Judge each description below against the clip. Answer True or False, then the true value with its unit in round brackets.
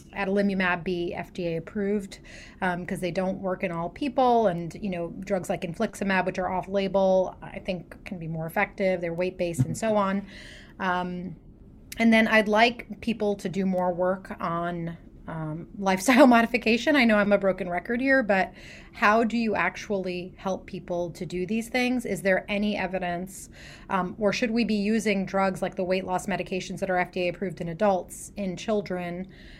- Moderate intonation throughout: False (2.3 semitones)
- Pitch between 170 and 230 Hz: True (190 Hz)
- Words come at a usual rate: True (180 wpm)